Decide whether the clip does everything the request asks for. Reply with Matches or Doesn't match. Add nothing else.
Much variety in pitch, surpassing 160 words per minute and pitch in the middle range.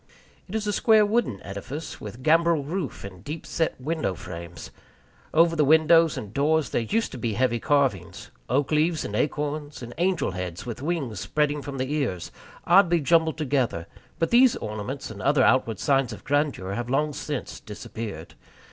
Matches